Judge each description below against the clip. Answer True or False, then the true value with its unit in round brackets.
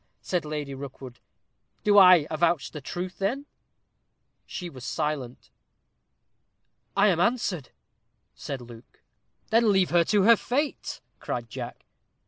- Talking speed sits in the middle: False (120 wpm)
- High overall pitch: False (175 Hz)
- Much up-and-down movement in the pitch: True (6.1 semitones)